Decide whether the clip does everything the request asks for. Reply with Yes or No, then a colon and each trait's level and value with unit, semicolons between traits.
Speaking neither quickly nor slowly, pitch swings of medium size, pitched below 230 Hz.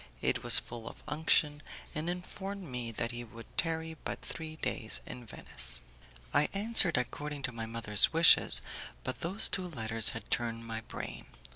No: average, 165 wpm; wide, 6.1 semitones; low, 135 Hz